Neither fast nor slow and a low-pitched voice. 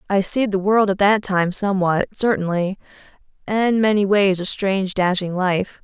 No: average, 165 wpm; high, 195 Hz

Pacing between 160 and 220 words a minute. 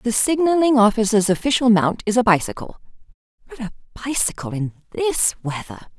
No: average, 140 wpm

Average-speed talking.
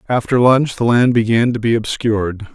Yes: average, 190 wpm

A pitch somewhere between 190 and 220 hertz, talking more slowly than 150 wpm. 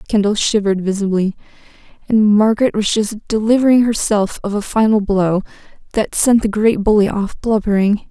Yes: high, 210 Hz; average, 140 wpm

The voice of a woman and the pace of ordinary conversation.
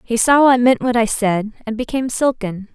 No: female; fast, 220 wpm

